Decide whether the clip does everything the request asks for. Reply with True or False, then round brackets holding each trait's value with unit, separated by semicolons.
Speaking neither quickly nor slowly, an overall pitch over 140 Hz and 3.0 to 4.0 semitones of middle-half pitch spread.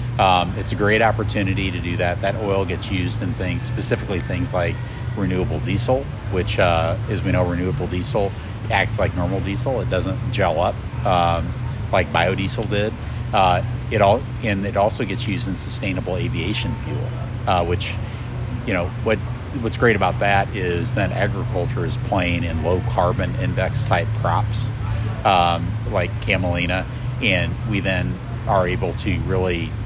False (160 wpm; 110 Hz; 3.4 semitones)